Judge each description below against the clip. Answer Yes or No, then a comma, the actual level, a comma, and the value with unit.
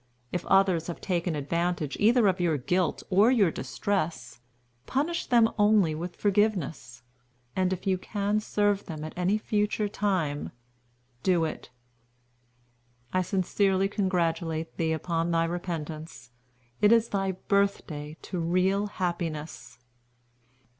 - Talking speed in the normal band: No, slow, 125 wpm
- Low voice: No, medium, 180 Hz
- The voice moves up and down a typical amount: Yes, average, 3.8 semitones